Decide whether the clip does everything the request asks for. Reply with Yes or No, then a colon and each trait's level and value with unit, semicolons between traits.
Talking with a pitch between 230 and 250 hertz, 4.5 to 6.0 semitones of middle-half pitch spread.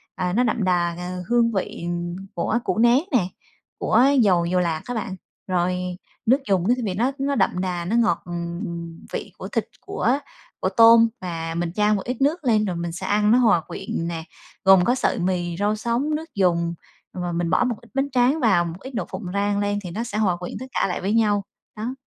No: high, 200 Hz; average, 5.1 semitones